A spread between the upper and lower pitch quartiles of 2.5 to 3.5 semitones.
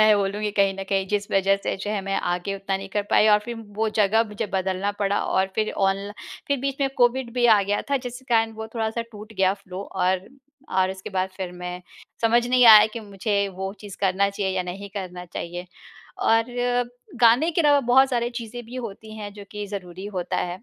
Yes: average, 2.9 semitones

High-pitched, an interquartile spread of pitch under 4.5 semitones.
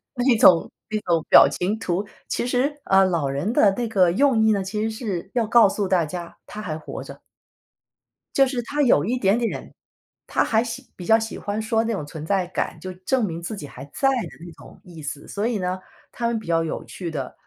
No: high, 205 Hz; average, 5.0 semitones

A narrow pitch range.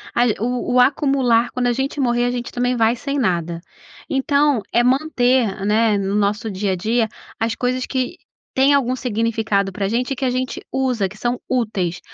No: average, 3.2 semitones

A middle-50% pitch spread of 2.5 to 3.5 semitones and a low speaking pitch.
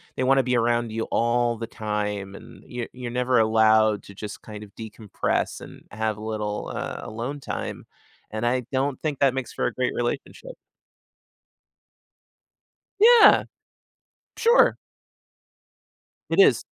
Yes: average, 2.9 semitones; low, 120 Hz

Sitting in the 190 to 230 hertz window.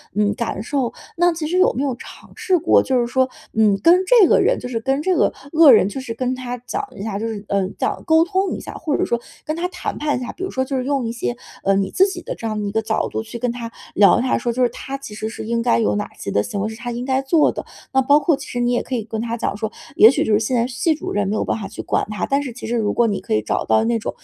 No: high, 240 Hz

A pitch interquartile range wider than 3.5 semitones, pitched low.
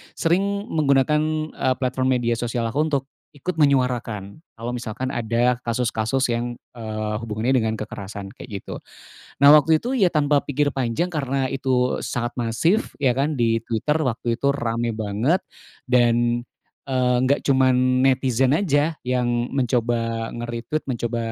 No: average, 2.9 semitones; low, 125 Hz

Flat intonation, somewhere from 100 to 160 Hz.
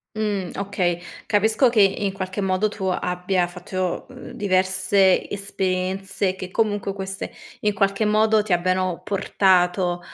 No: narrow, 1.8 semitones; high, 195 Hz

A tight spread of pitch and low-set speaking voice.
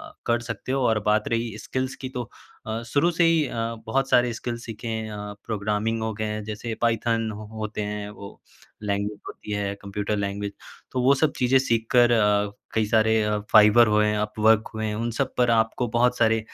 Yes: narrow, 2.1 semitones; low, 110 Hz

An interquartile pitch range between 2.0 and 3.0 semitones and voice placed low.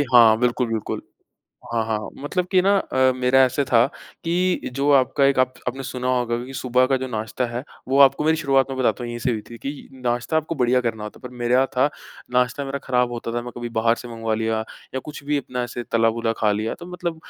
Yes: narrow, 2.5 semitones; low, 125 Hz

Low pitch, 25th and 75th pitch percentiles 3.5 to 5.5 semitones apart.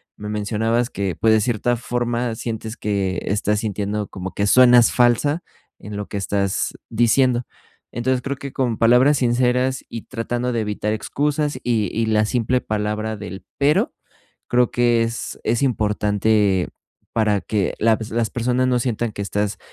No: low, 115 Hz; average, 2.7 semitones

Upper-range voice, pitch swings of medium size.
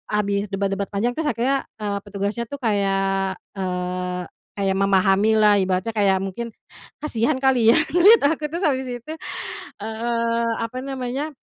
Yes: high, 215 Hz; average, 4.2 semitones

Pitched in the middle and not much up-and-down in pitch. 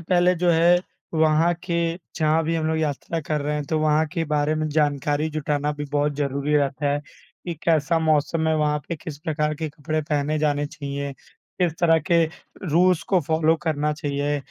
Yes: medium, 155 Hz; narrow, 1.8 semitones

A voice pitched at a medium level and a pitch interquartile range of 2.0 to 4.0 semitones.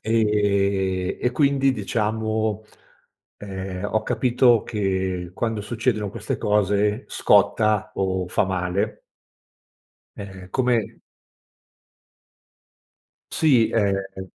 No: low, 105 Hz; narrow, 2.6 semitones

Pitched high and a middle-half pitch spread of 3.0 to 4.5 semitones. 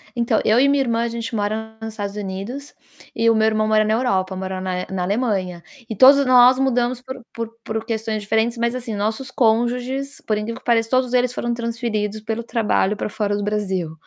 No: high, 225 Hz; narrow, 2.6 semitones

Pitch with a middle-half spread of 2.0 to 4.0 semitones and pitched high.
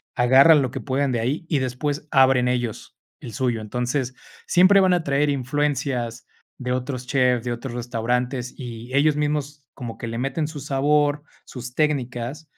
No: average, 3.0 semitones; low, 130 Hz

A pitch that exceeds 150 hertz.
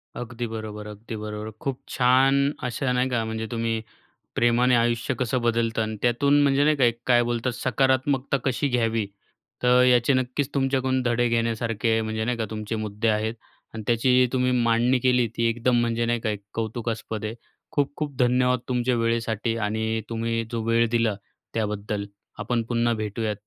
No: low, 115 Hz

